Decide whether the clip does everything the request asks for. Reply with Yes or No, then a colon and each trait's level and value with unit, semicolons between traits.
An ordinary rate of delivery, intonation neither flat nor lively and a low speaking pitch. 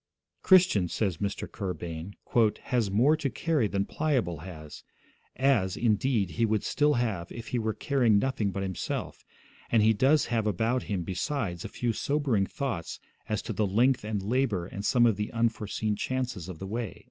Yes: average, 180 wpm; average, 4.6 semitones; low, 110 Hz